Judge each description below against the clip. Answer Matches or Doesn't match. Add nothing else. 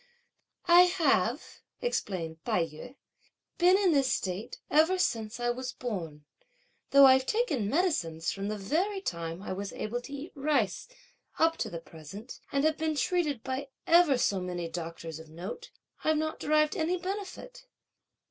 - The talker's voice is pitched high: Matches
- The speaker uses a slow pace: Doesn't match